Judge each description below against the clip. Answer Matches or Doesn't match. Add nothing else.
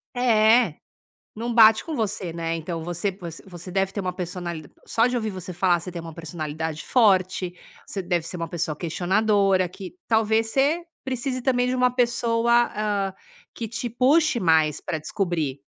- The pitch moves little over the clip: Doesn't match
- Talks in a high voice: Matches